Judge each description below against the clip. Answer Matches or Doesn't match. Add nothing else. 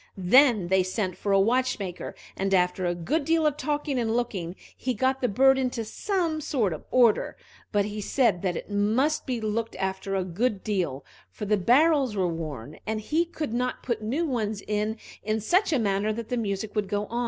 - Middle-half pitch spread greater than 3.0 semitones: Matches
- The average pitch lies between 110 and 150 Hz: Doesn't match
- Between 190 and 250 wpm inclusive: Matches